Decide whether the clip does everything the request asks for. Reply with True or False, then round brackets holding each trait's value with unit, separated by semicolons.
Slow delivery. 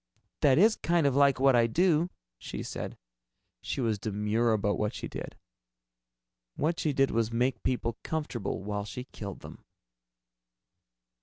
False (150 wpm)